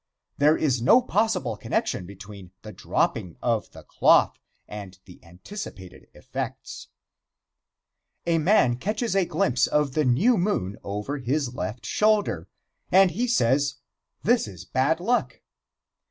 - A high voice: No, low, 135 Hz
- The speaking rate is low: Yes, slow, 130 wpm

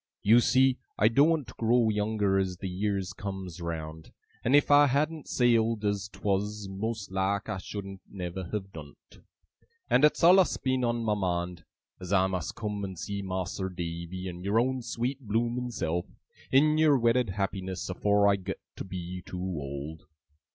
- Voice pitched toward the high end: No, low, 100 Hz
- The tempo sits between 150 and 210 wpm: Yes, average, 170 wpm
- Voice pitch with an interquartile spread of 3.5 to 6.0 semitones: Yes, average, 4.2 semitones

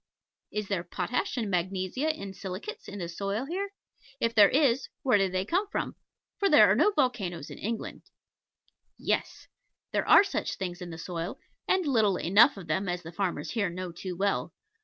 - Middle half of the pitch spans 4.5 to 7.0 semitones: Yes, wide, 5.5 semitones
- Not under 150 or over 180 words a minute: No, average, 190 wpm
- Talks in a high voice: Yes, high, 200 Hz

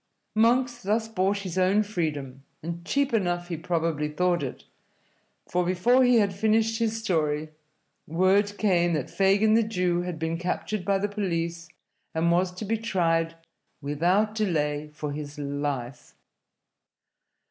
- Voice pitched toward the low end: No, medium, 180 Hz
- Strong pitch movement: No, average, 4.5 semitones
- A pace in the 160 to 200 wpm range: No, average, 145 wpm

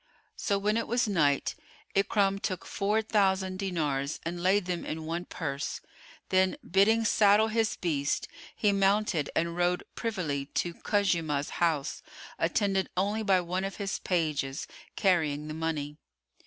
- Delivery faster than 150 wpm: No, average, 140 wpm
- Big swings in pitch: No, average, 3.9 semitones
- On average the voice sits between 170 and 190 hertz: Yes, medium, 185 Hz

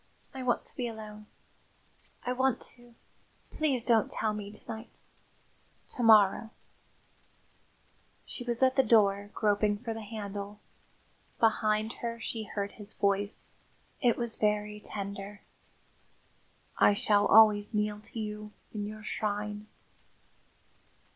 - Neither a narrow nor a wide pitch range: No, narrow, 1.8 semitones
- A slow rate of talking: Yes, slow, 130 wpm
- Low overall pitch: No, high, 215 Hz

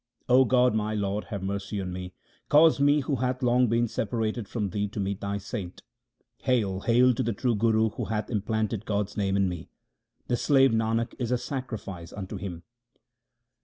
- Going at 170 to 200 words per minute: Yes, average, 185 wpm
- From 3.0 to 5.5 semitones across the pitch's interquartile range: Yes, average, 3.6 semitones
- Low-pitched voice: Yes, low, 110 Hz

